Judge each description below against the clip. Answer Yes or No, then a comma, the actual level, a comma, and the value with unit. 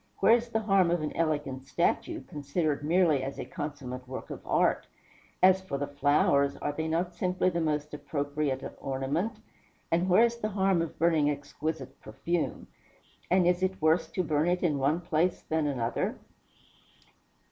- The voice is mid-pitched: Yes, medium, 155 Hz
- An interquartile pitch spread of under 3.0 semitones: No, average, 4.0 semitones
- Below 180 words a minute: Yes, average, 170 wpm